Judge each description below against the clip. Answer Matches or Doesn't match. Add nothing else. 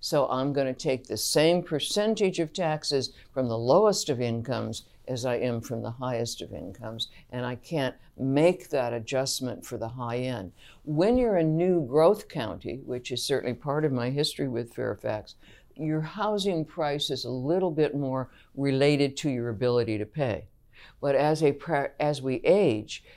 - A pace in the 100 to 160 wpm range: Doesn't match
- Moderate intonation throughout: Matches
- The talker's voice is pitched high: Doesn't match